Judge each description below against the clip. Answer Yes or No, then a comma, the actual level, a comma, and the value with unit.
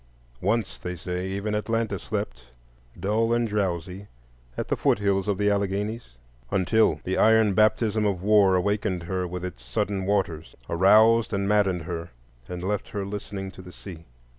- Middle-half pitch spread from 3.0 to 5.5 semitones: No, narrow, 2.6 semitones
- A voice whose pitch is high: No, low, 100 Hz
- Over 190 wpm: No, average, 165 wpm